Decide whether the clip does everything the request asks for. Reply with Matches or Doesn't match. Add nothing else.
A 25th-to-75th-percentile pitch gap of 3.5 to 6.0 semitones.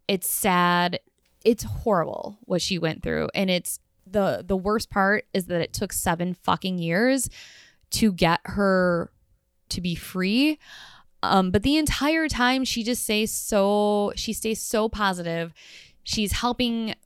Matches